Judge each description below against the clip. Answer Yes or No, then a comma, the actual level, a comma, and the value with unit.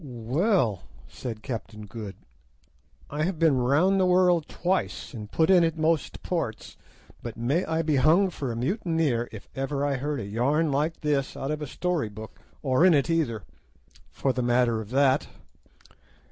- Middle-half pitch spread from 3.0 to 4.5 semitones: No, wide, 5.4 semitones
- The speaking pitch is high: No, medium, 140 Hz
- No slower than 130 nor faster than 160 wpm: No, average, 175 wpm